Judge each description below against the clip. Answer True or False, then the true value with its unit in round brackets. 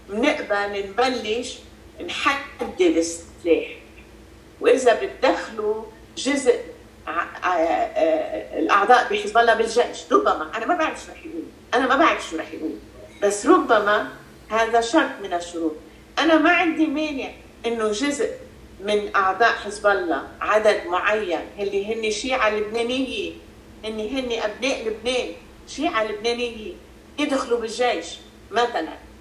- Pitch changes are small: False (5.6 semitones)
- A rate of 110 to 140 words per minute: True (125 wpm)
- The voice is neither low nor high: False (235 Hz)